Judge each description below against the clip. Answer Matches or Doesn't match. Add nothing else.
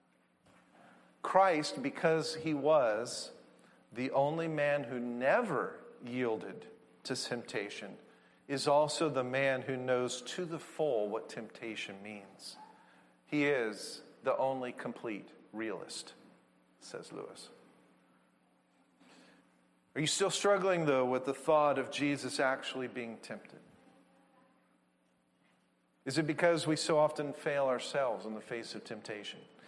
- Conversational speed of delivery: Doesn't match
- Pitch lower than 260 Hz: Matches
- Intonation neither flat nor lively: Doesn't match